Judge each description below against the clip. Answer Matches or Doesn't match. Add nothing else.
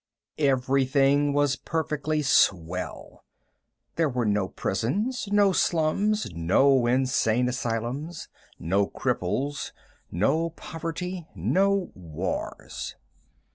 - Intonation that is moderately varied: Doesn't match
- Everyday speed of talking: Doesn't match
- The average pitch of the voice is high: Doesn't match